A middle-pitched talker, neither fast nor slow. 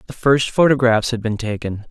No: low, 120 Hz; average, 190 wpm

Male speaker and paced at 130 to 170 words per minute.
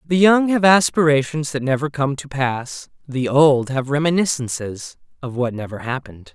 Yes: male; average, 160 wpm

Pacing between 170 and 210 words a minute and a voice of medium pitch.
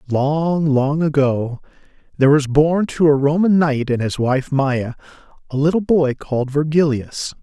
No: average, 155 wpm; medium, 145 Hz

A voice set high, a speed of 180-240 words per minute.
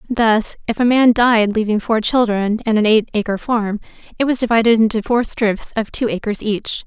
Yes: high, 225 Hz; average, 200 wpm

